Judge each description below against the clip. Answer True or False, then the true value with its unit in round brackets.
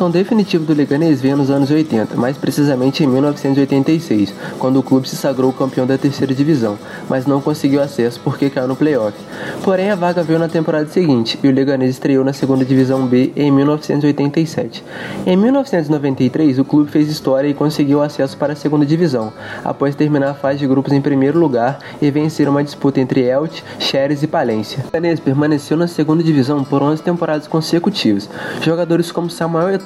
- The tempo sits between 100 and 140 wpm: False (180 wpm)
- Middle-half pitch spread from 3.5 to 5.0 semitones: False (2.8 semitones)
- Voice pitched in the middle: True (145 Hz)